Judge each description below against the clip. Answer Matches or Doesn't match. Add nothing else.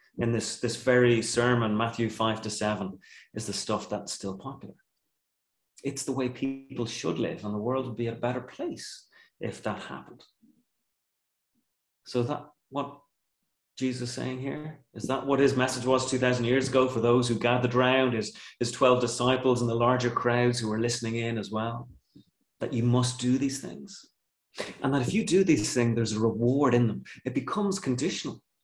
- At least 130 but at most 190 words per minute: Matches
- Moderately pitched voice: Doesn't match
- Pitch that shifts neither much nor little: Doesn't match